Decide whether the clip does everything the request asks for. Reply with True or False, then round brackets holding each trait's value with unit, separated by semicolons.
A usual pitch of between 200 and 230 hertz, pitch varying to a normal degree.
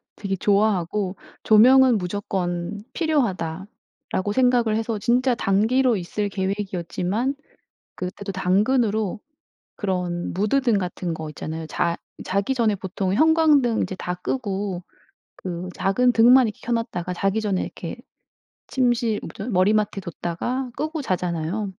True (205 Hz; 4.6 semitones)